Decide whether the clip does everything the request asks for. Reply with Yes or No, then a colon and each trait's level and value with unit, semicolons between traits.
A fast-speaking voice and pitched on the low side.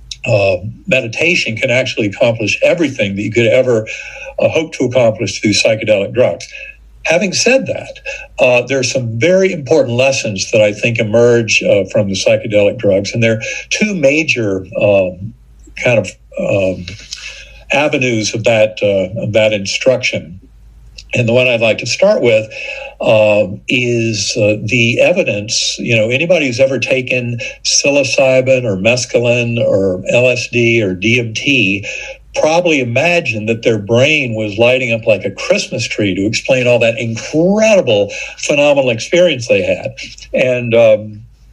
No: average, 145 wpm; low, 120 Hz